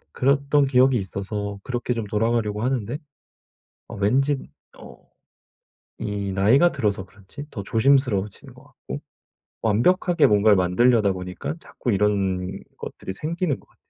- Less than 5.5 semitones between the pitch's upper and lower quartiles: Yes, average, 5.1 semitones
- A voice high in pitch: No, low, 110 Hz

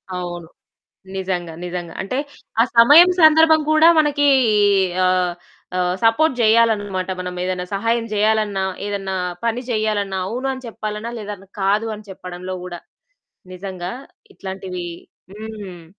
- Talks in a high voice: Yes, high, 205 Hz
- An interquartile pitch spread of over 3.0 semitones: Yes, average, 3.9 semitones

